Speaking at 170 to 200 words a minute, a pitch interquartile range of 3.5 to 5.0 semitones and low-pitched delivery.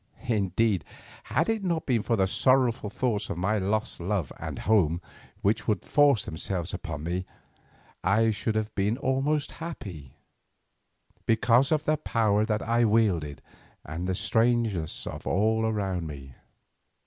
No: average, 145 wpm; average, 4.3 semitones; low, 110 Hz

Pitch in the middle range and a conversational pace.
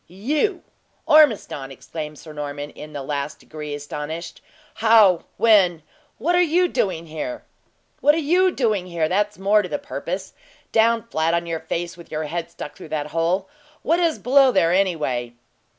Yes: medium, 175 Hz; average, 165 wpm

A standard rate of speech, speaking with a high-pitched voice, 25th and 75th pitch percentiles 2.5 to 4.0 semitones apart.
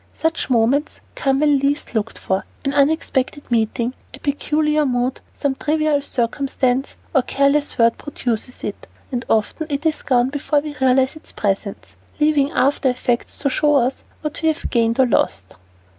Yes: average, 160 wpm; very high, 275 Hz; average, 3.3 semitones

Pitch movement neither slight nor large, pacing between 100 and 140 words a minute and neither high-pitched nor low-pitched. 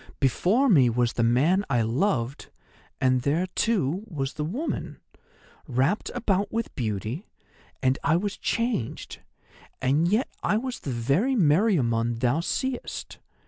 No: wide, 8.7 semitones; slow, 135 wpm; medium, 150 Hz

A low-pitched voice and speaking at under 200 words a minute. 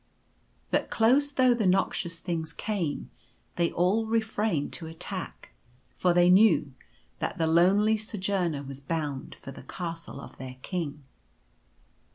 No: medium, 175 Hz; average, 140 wpm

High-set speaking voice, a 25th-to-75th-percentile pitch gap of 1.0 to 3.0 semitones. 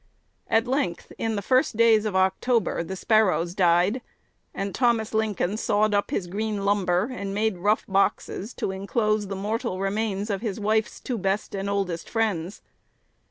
Yes: high, 205 Hz; narrow, 2.5 semitones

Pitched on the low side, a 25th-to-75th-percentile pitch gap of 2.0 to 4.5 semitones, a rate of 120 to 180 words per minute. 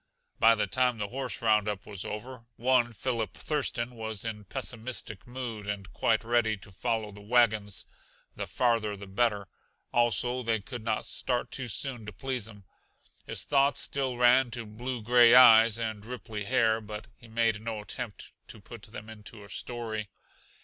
Yes: low, 115 Hz; narrow, 2.6 semitones; average, 170 wpm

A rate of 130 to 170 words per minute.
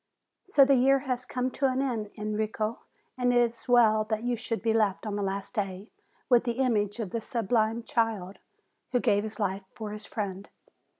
No: average, 195 wpm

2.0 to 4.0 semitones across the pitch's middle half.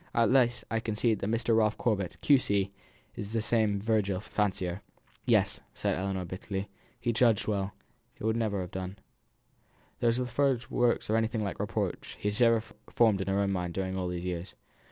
Yes: average, 3.1 semitones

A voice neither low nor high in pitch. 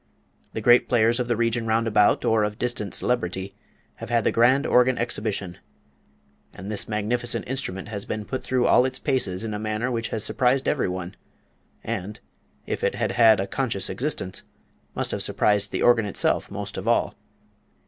No: low, 115 Hz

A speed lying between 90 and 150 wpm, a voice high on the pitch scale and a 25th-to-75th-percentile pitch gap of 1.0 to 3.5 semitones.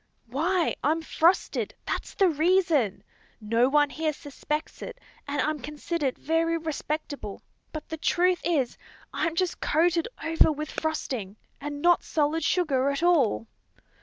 Yes: slow, 135 wpm; very high, 310 Hz; average, 2.9 semitones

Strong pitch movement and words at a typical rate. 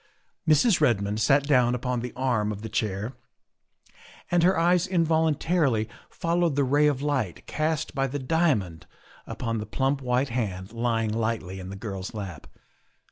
Yes: wide, 5.8 semitones; average, 155 wpm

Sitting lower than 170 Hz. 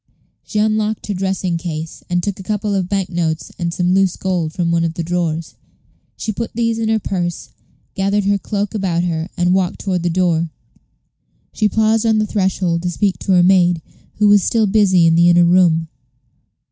No: medium, 185 Hz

